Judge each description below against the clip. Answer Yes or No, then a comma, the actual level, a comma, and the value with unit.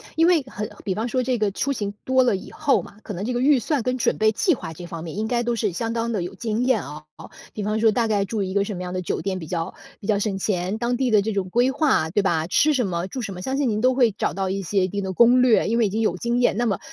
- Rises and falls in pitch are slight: No, average, 4.3 semitones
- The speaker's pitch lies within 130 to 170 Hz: No, high, 215 Hz